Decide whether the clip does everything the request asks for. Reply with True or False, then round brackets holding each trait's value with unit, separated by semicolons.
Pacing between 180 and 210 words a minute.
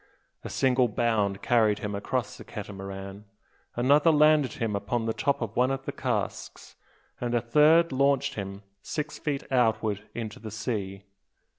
False (155 wpm)